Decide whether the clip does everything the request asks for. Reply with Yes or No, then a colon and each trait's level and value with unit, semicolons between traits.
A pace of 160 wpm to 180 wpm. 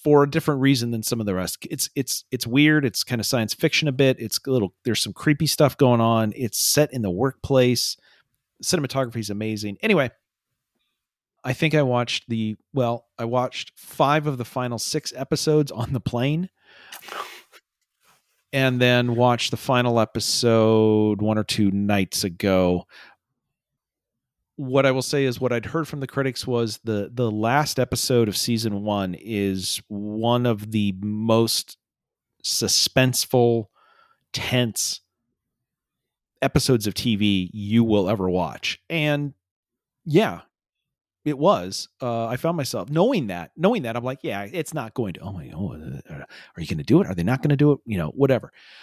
Yes: average, 170 wpm